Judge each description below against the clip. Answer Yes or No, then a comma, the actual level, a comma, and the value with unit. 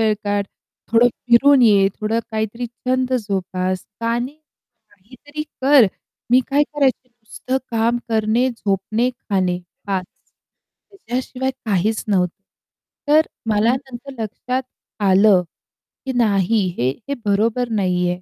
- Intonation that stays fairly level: No, average, 4.2 semitones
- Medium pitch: No, high, 225 Hz